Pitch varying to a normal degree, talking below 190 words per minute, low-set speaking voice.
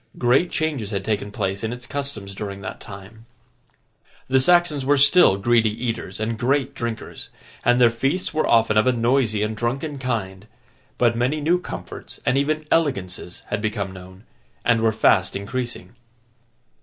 Yes: average, 4.4 semitones; average, 160 wpm; low, 115 Hz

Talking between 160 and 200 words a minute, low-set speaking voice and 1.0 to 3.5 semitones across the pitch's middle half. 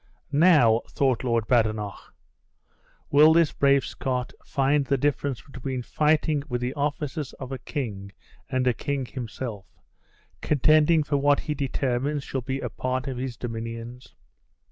No: average, 145 wpm; low, 130 Hz; average, 2.9 semitones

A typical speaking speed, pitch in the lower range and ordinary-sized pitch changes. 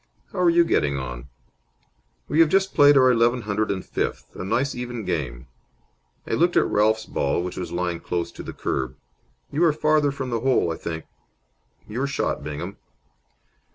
No: average, 180 wpm; low, 110 Hz; wide, 8.7 semitones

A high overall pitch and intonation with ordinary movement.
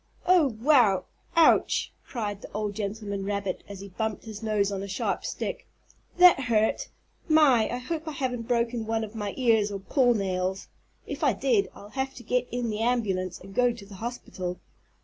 Yes: high, 220 Hz; average, 3.7 semitones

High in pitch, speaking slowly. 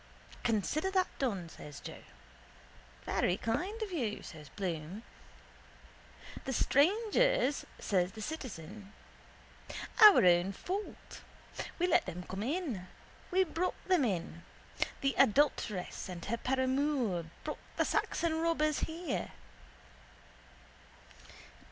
Yes: very high, 260 Hz; slow, 105 wpm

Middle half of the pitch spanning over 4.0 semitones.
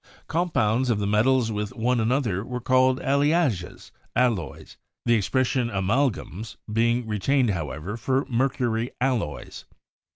No: average, 3.6 semitones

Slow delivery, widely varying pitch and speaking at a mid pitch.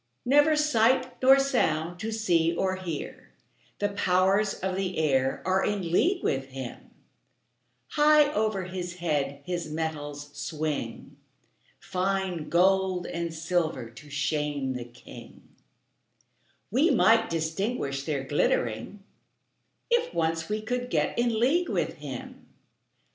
Yes: slow, 120 wpm; wide, 6.4 semitones; medium, 180 Hz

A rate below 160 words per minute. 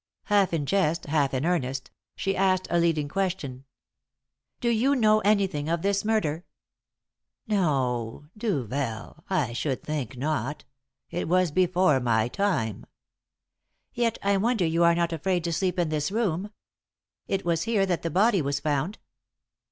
Yes: average, 150 wpm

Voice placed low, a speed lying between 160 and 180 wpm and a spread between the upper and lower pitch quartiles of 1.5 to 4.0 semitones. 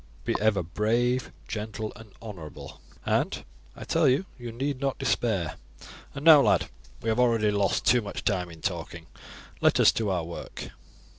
No: low, 110 Hz; average, 165 wpm; average, 4.4 semitones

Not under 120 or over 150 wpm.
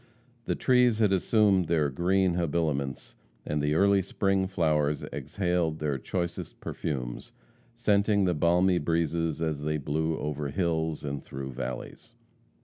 Yes: slow, 135 wpm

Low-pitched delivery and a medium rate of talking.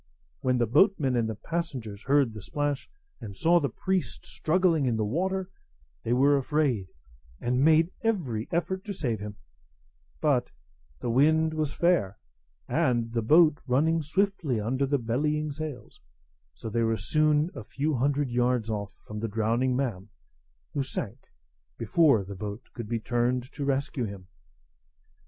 Yes: low, 130 Hz; average, 150 wpm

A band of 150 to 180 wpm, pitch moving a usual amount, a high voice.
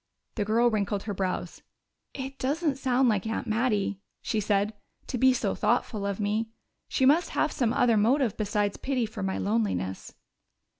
Yes: average, 165 wpm; average, 4.1 semitones; high, 215 Hz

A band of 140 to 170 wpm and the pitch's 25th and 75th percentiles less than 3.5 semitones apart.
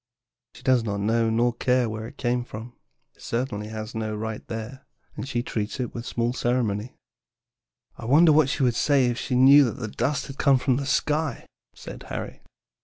No: fast, 205 wpm; average, 2.9 semitones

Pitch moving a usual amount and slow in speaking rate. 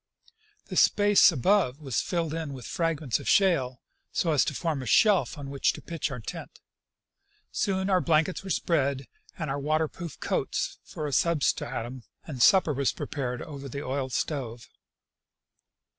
No: average, 4.0 semitones; average, 165 wpm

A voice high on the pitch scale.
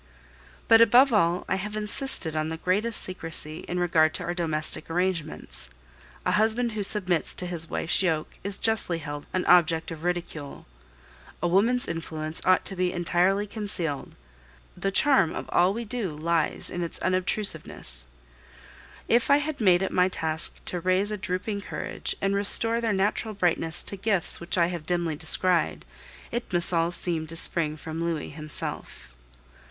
No: medium, 180 Hz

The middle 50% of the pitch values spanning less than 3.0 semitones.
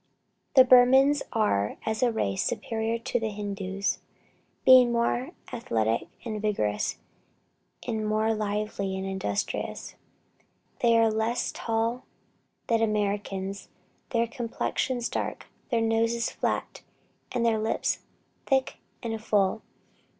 Yes: narrow, 2.4 semitones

